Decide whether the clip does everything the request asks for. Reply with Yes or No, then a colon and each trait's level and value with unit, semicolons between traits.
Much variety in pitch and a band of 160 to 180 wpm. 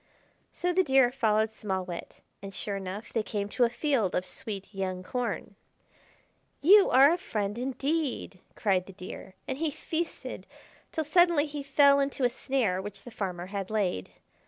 Yes: wide, 6.3 semitones; average, 170 wpm